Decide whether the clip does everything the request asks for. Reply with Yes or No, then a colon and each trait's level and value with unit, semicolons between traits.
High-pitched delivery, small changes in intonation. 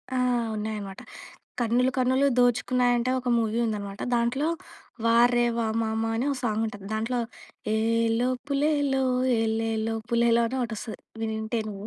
Yes: high, 230 Hz; narrow, 2.0 semitones